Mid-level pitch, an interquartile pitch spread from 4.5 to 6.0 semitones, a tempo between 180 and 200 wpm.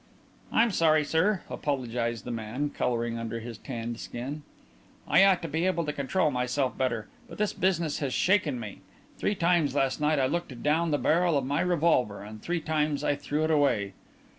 Yes: medium, 145 Hz; wide, 5.4 semitones; average, 190 wpm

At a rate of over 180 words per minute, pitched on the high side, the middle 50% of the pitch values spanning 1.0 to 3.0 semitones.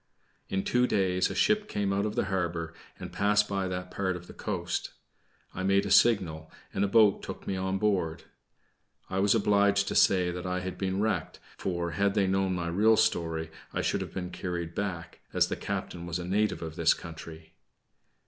No: average, 200 wpm; very low, 95 Hz; narrow, 2.6 semitones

